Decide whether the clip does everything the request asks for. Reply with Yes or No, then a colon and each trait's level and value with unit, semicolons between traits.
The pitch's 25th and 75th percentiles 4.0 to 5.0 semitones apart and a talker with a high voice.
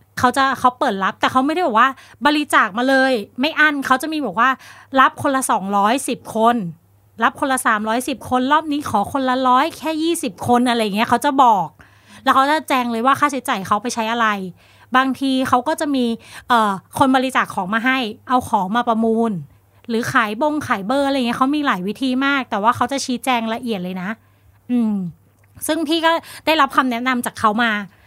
No: average, 3.4 semitones; very high, 255 Hz